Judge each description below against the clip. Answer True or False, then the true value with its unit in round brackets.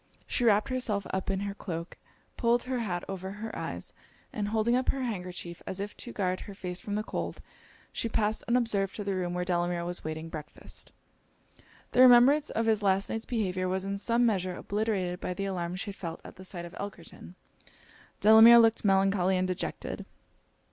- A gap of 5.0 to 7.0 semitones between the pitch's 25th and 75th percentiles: False (3.5 semitones)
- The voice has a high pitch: True (195 Hz)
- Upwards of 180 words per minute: True (190 wpm)